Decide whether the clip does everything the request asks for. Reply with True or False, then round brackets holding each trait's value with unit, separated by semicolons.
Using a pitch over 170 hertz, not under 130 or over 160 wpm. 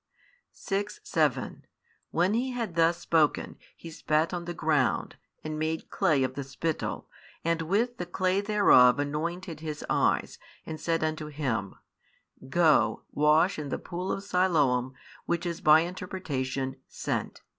False (160 Hz; 145 wpm)